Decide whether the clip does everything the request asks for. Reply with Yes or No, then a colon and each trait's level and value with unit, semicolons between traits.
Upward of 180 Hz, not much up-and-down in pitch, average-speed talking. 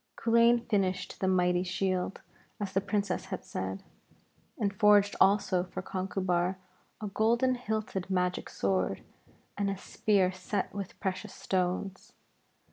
No: high, 190 Hz; narrow, 2.1 semitones; slow, 125 wpm